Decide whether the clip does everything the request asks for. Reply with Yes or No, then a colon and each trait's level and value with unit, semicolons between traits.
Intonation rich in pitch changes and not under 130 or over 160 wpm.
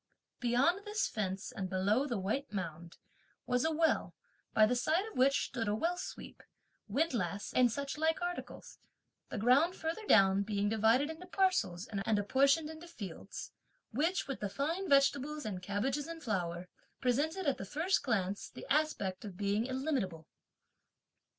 Yes: wide, 7.7 semitones; average, 155 wpm